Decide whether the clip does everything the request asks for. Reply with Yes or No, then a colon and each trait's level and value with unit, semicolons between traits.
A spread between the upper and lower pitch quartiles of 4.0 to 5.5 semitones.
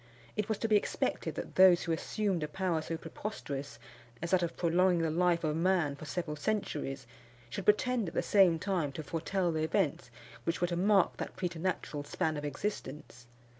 No: average, 3.4 semitones